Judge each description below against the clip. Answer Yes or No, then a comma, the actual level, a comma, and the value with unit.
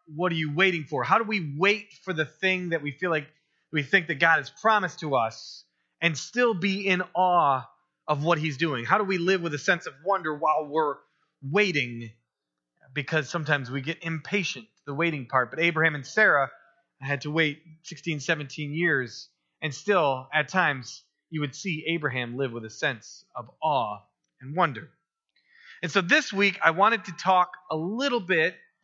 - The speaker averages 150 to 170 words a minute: No, average, 185 wpm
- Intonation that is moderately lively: Yes, average, 4.2 semitones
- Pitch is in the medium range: Yes, medium, 160 Hz